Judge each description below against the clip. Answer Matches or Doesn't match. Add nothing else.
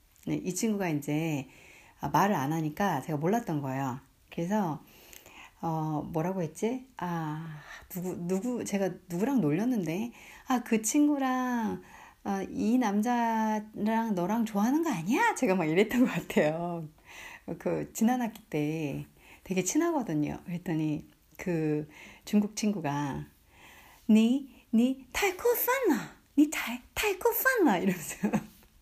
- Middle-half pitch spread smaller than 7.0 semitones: Doesn't match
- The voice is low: Doesn't match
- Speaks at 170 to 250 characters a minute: Matches